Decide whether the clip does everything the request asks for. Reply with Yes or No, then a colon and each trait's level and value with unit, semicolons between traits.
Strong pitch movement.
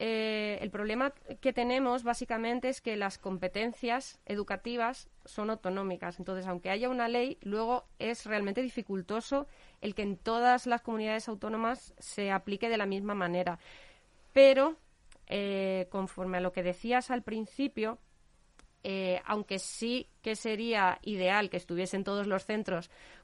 No: average, 3.8 semitones